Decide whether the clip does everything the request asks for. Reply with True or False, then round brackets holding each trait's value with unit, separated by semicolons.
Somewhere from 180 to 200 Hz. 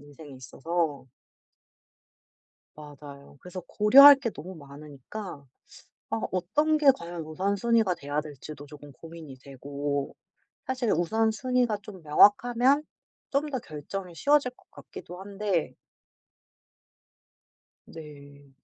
False (170 Hz)